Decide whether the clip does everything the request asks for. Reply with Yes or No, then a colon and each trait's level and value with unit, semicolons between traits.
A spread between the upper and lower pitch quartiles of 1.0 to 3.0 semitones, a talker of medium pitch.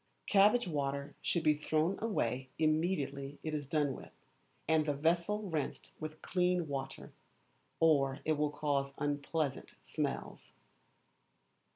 Yes: average, 2.7 semitones; medium, 155 Hz